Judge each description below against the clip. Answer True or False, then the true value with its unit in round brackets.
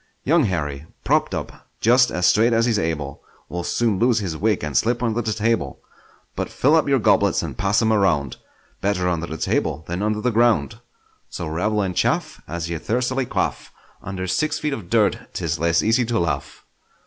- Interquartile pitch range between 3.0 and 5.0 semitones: False (5.6 semitones)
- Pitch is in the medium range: False (105 Hz)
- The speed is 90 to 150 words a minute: False (195 wpm)